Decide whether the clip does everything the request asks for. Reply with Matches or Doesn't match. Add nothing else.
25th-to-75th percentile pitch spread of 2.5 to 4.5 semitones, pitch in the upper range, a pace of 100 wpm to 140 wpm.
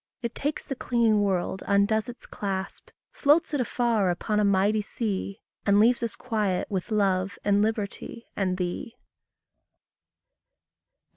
Matches